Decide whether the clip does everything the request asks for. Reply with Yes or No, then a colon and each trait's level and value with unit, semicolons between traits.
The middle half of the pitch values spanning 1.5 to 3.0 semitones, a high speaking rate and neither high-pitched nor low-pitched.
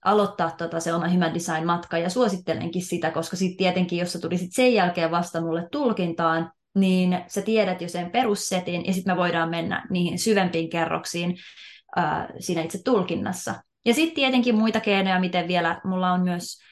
Yes: narrow, 2.6 semitones; fast, 170 wpm; medium, 180 Hz